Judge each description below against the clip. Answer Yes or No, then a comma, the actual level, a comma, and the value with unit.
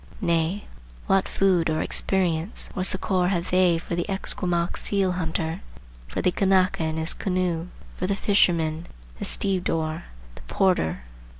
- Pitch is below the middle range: No, medium, 180 Hz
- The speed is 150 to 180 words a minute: No, average, 140 wpm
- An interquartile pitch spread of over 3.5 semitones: No, narrow, 2.5 semitones